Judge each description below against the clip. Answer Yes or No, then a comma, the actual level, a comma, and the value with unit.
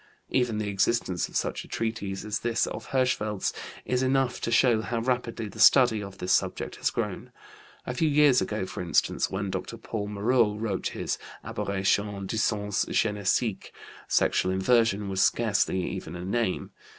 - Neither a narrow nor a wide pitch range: Yes, average, 3.2 semitones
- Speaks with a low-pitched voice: Yes, low, 105 Hz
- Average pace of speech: Yes, average, 165 wpm